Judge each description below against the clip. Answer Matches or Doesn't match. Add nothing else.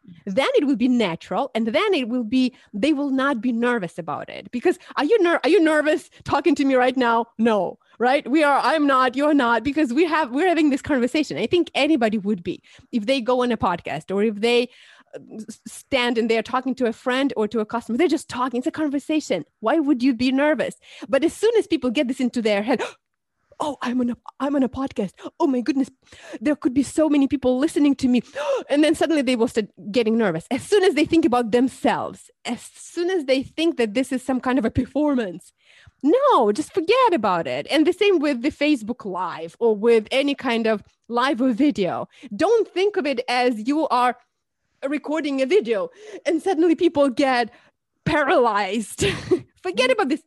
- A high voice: Matches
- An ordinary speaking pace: Doesn't match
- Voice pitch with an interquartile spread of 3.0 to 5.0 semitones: Matches